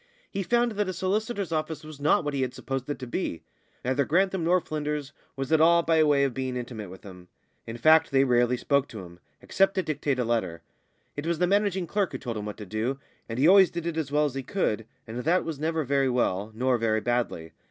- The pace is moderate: No, fast, 240 wpm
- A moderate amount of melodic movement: No, wide, 5.7 semitones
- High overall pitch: No, medium, 140 Hz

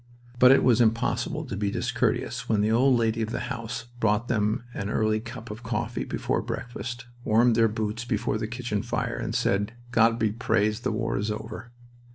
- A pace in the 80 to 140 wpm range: No, average, 190 wpm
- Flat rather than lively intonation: Yes, narrow, 1.7 semitones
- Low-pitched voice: Yes, low, 115 Hz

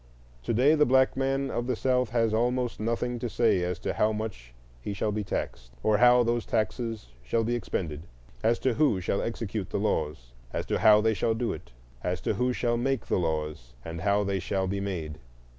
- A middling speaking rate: No, fast, 210 wpm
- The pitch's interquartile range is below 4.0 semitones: No, average, 4.7 semitones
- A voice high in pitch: No, low, 110 Hz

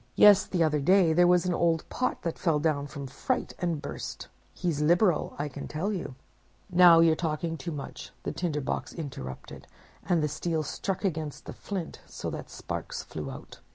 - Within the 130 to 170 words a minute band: No, average, 185 wpm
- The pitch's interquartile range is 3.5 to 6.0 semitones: No, average, 3.0 semitones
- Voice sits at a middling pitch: Yes, medium, 165 Hz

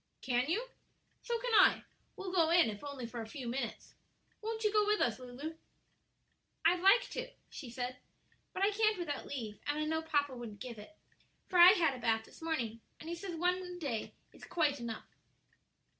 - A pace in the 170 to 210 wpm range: Yes, average, 200 wpm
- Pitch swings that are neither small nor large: No, wide, 6.9 semitones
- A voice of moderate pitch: No, very high, 305 Hz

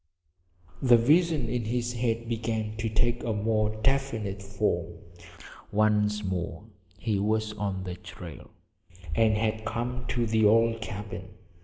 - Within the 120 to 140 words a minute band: Yes, slow, 135 wpm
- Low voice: Yes, low, 110 Hz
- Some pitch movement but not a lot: No, narrow, 2.0 semitones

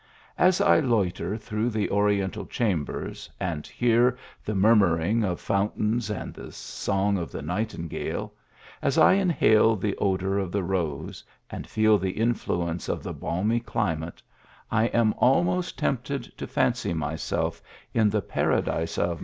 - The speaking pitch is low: Yes, low, 105 Hz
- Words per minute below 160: Yes, average, 145 wpm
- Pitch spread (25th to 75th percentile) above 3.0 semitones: Yes, average, 4.4 semitones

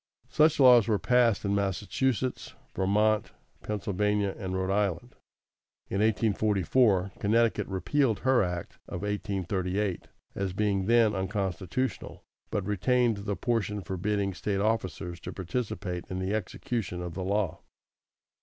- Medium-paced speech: No, slow, 125 wpm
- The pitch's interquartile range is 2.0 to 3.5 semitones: Yes, average, 2.9 semitones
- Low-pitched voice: Yes, low, 100 Hz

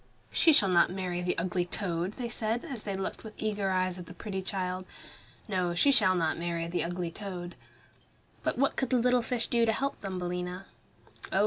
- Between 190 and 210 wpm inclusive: Yes, average, 200 wpm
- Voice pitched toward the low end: No, medium, 185 Hz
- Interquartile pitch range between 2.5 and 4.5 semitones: Yes, average, 3.5 semitones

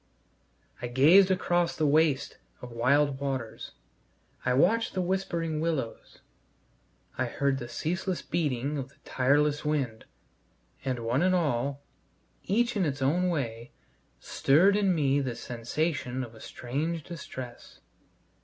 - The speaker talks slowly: Yes, slow, 130 wpm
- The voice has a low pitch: No, medium, 145 Hz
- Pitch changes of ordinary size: Yes, average, 4.9 semitones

